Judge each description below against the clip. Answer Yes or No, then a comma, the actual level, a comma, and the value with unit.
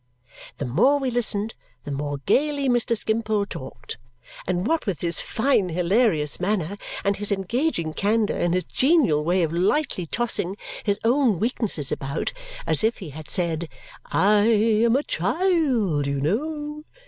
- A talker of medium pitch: No, high, 205 Hz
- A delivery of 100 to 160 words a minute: Yes, average, 150 wpm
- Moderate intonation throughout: No, wide, 6.2 semitones